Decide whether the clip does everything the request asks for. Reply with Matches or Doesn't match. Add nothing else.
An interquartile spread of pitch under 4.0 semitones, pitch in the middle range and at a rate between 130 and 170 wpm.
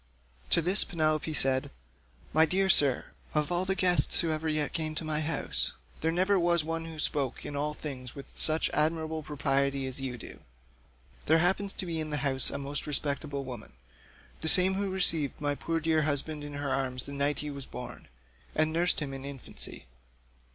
Doesn't match